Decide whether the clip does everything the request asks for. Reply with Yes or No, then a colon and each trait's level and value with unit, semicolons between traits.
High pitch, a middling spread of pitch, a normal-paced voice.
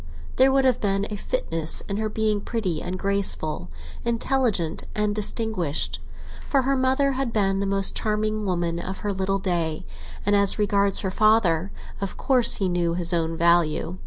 Yes: high, 200 Hz; average, 3.8 semitones; average, 170 wpm